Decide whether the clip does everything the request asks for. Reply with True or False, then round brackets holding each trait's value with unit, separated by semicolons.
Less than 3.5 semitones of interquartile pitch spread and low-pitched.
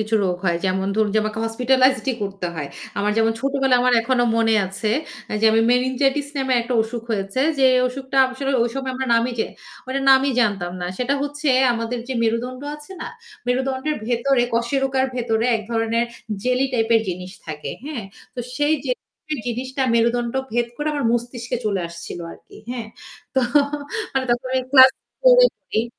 False (2.9 semitones; 245 Hz)